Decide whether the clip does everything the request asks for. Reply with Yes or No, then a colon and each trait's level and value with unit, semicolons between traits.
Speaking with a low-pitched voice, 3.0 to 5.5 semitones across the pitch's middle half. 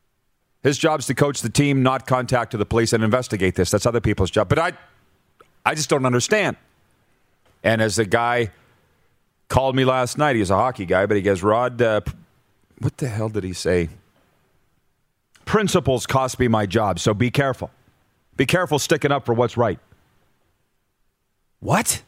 Yes: low, 120 Hz; average, 4.2 semitones